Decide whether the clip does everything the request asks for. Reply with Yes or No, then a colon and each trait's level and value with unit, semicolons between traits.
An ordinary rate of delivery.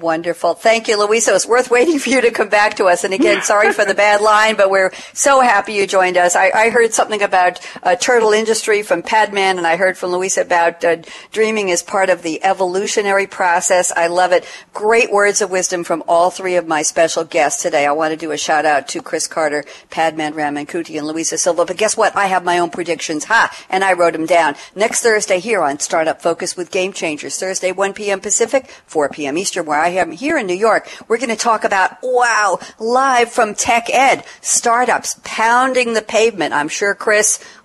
No: fast, 210 wpm